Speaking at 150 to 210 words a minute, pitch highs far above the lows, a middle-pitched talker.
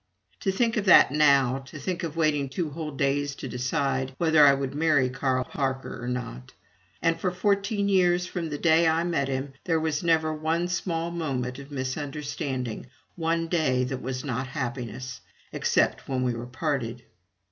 No: average, 175 wpm; average, 4.2 semitones; medium, 145 Hz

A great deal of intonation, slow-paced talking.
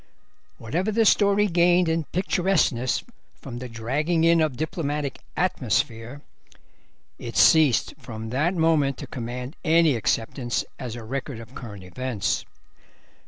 Yes: wide, 5.7 semitones; slow, 125 wpm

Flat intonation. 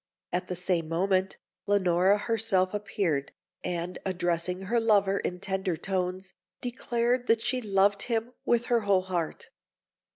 No: average, 3.6 semitones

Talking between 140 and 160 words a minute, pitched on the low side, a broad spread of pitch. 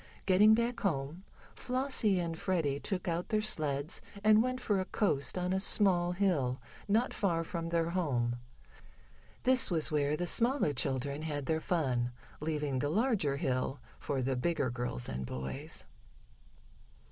No: average, 150 wpm; medium, 165 Hz; wide, 5.9 semitones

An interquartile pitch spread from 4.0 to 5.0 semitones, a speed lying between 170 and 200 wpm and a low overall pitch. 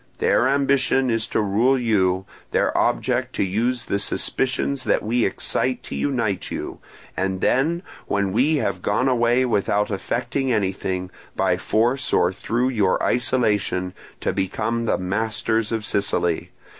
No: average, 4.5 semitones; average, 145 wpm; low, 115 Hz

